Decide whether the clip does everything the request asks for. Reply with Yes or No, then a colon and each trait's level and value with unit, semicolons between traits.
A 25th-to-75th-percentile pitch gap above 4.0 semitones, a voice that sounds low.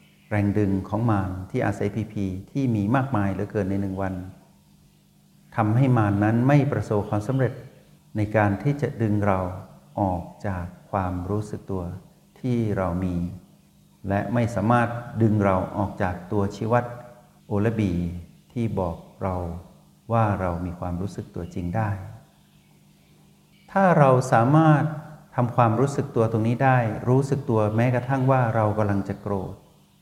Yes: average, 4.6 semitones; low, 110 Hz